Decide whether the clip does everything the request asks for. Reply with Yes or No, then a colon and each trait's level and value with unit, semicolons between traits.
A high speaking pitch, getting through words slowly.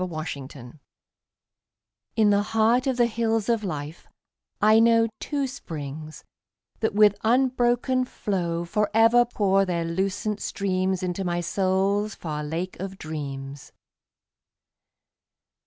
Yes: high, 195 Hz; slow, 115 wpm